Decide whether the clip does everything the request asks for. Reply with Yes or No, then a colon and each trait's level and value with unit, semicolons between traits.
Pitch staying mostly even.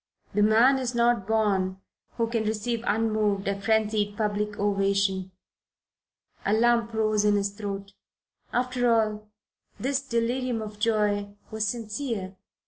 Yes: narrow, 2.3 semitones